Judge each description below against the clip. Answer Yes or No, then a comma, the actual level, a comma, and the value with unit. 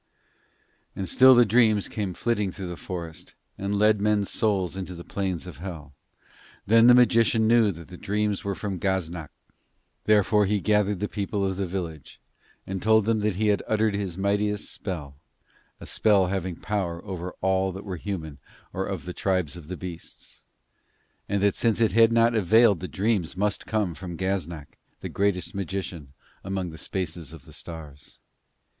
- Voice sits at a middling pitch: No, very low, 95 Hz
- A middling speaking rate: Yes, average, 175 wpm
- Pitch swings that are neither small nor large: Yes, average, 3.0 semitones